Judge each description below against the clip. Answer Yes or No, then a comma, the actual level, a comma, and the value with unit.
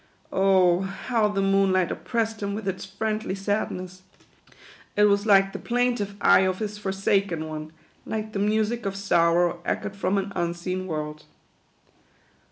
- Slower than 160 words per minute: Yes, average, 150 wpm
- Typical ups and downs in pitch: No, narrow, 2.2 semitones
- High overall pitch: Yes, high, 195 Hz